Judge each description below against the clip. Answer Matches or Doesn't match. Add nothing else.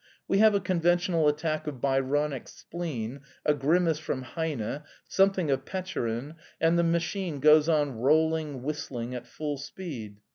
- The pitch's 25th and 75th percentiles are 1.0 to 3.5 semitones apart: Doesn't match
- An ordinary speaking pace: Matches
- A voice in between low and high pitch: Matches